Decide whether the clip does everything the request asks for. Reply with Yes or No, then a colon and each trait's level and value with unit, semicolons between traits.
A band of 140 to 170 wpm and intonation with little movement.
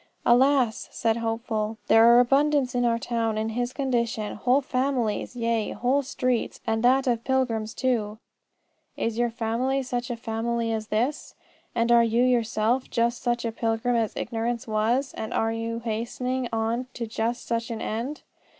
Yes: average, 165 wpm; narrow, 1.9 semitones